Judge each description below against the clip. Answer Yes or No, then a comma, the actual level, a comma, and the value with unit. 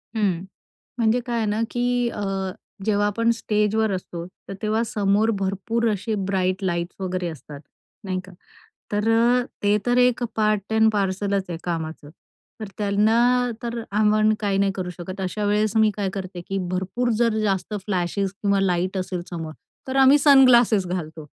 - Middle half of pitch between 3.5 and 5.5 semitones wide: No, average, 2.9 semitones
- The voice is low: No, high, 205 Hz